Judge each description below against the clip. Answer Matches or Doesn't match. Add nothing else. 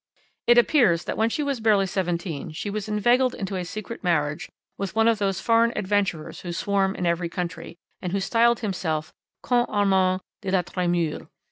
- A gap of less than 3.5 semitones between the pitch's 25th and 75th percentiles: Doesn't match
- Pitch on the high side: Matches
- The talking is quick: Doesn't match